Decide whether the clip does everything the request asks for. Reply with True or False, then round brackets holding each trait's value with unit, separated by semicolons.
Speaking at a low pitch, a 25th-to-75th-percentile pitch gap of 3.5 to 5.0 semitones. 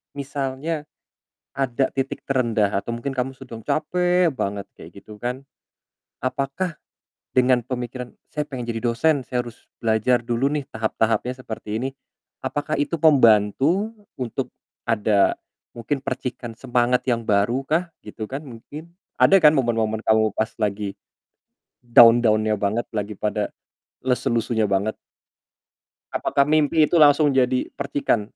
True (125 Hz; 4.1 semitones)